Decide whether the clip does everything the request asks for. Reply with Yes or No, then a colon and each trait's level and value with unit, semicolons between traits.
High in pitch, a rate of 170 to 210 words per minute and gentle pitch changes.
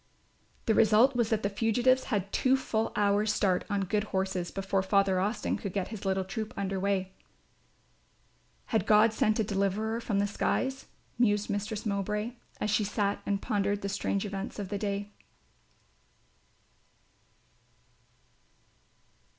No: high, 205 Hz; average, 140 wpm; narrow, 1.7 semitones